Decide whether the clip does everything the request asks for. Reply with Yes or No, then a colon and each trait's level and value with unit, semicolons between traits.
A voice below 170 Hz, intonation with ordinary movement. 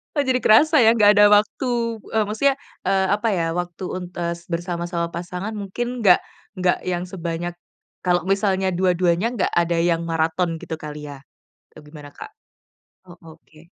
No: medium, 180 Hz; average, 3.5 semitones